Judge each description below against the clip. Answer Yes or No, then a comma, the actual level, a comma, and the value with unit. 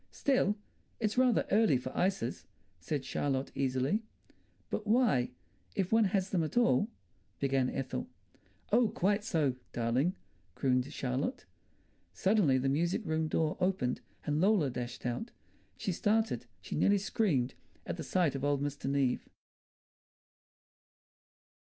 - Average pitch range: No, wide, 7.5 semitones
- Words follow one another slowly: Yes, slow, 130 wpm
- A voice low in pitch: No, medium, 155 Hz